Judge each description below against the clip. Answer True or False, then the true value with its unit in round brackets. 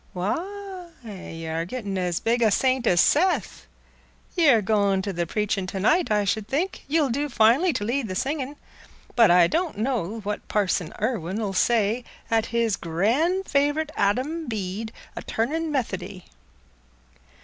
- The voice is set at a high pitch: True (225 Hz)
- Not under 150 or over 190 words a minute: True (160 wpm)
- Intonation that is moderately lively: False (6.5 semitones)